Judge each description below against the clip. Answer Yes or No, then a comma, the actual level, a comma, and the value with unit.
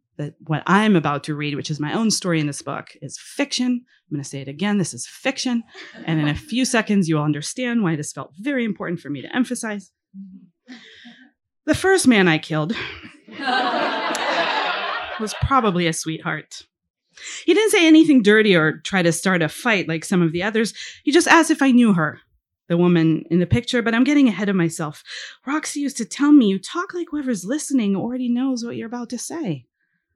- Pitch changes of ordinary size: No, wide, 7.8 semitones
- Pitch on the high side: Yes, high, 205 Hz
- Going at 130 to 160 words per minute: No, average, 200 wpm